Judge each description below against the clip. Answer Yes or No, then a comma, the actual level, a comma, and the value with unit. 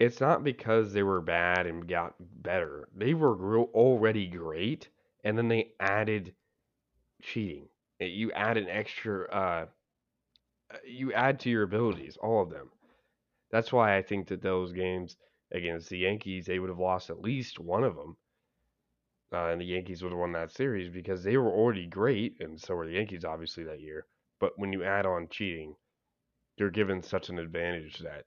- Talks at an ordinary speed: Yes, average, 180 wpm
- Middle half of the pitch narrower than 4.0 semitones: No, average, 4.3 semitones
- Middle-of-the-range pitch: No, very low, 95 Hz